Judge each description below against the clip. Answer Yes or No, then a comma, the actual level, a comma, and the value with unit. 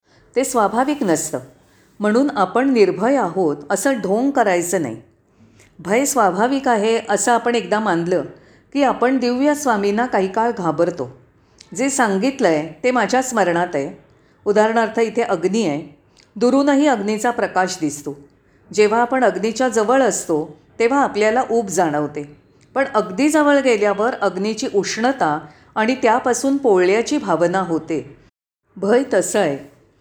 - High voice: Yes, high, 215 Hz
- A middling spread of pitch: No, wide, 6.0 semitones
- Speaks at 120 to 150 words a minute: Yes, average, 125 wpm